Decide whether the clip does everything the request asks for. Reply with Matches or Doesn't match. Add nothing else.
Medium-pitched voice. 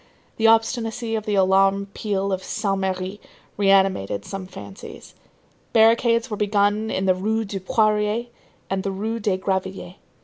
Doesn't match